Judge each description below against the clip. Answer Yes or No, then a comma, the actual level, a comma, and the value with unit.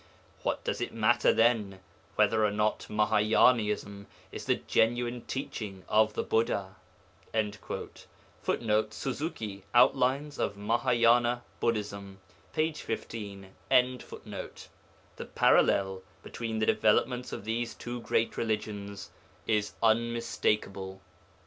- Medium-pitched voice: No, low, 110 Hz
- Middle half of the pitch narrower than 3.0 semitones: Yes, narrow, 2.6 semitones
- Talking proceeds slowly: Yes, slow, 100 wpm